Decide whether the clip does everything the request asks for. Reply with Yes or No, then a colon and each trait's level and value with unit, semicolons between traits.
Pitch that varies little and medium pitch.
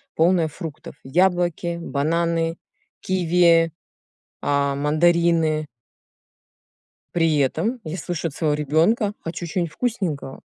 Yes: narrow, 2.2 semitones; medium, 165 Hz